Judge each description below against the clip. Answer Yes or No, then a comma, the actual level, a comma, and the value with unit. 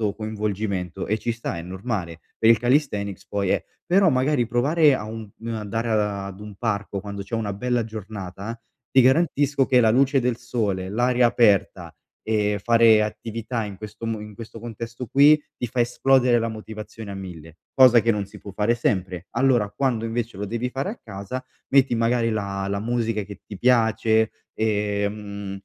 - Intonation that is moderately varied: Yes, average, 3.0 semitones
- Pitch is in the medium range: No, low, 110 Hz